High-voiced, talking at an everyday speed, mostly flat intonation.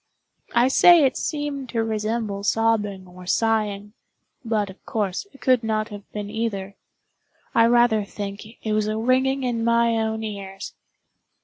Yes: high, 220 Hz; average, 145 wpm; narrow, 2.3 semitones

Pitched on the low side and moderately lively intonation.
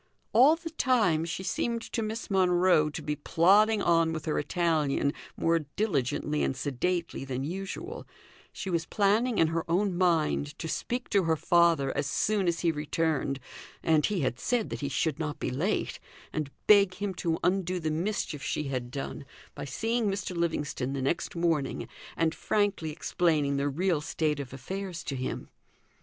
No: medium, 165 Hz; average, 4.6 semitones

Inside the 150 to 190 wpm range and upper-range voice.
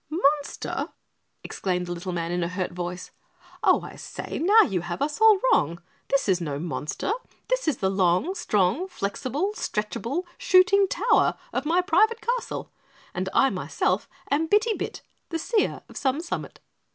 Yes: average, 165 wpm; very high, 280 Hz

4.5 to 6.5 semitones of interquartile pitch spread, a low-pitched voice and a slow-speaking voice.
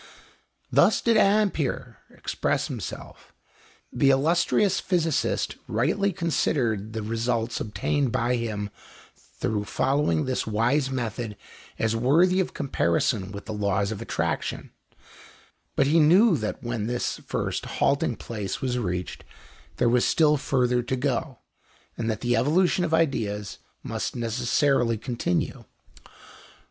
Yes: average, 5.1 semitones; low, 125 Hz; slow, 125 wpm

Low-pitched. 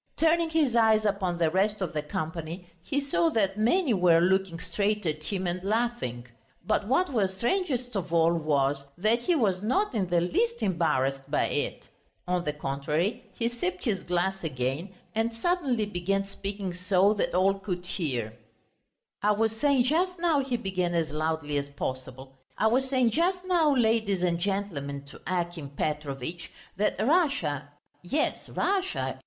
No: high, 195 Hz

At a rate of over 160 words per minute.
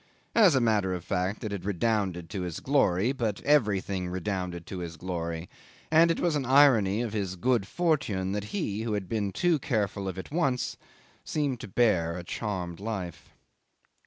Yes: average, 180 wpm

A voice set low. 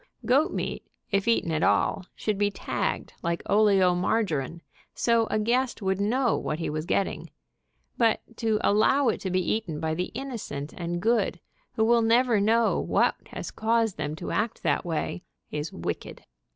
No: high, 205 Hz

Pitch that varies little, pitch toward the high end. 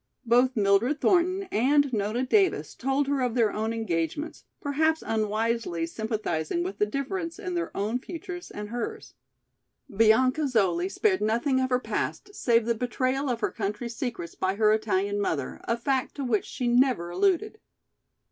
No: average, 5.0 semitones; high, 240 Hz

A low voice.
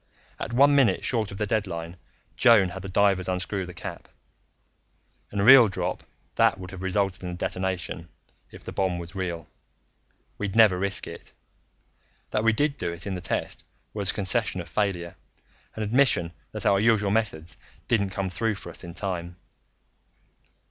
Yes: very low, 95 Hz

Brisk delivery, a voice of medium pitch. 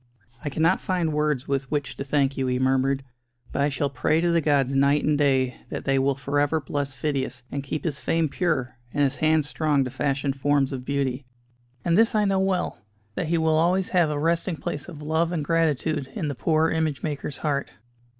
Yes: fast, 215 wpm; medium, 145 Hz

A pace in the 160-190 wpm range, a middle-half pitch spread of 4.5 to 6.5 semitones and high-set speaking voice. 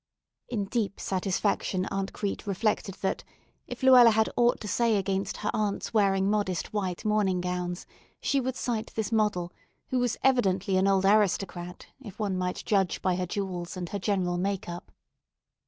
No: average, 170 wpm; average, 2.7 semitones; high, 195 Hz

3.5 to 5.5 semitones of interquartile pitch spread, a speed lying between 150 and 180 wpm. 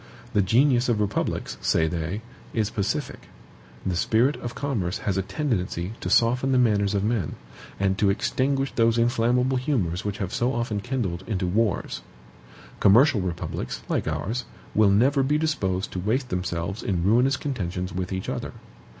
Yes: average, 4.9 semitones; average, 160 wpm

